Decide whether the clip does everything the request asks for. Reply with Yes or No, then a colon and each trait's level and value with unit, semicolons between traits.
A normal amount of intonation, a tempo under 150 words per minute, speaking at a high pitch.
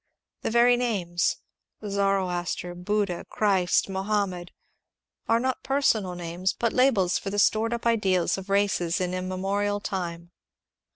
Yes: average, 3.1 semitones; slow, 135 wpm; high, 195 Hz